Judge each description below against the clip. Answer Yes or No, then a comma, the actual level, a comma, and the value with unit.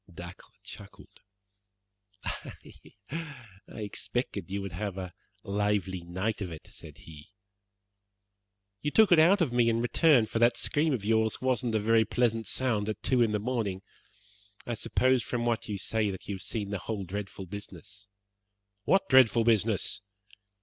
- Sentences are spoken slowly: No, average, 160 wpm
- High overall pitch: No, low, 110 Hz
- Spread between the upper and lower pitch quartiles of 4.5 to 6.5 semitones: No, average, 3.4 semitones